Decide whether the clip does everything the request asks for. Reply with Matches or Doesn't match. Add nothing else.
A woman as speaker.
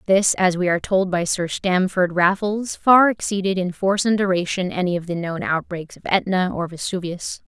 Matches